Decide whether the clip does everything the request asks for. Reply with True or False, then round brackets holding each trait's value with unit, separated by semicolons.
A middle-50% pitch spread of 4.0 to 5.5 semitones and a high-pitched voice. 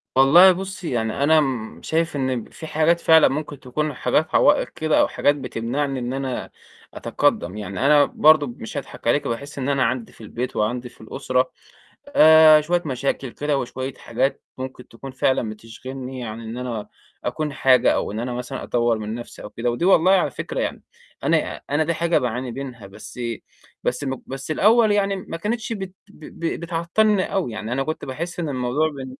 False (4.4 semitones; 135 Hz)